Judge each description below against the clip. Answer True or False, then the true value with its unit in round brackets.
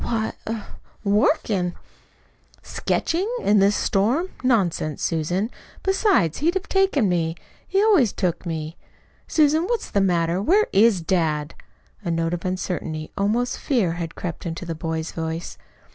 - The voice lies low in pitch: False (190 Hz)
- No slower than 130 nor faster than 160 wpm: True (140 wpm)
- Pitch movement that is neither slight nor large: False (7.1 semitones)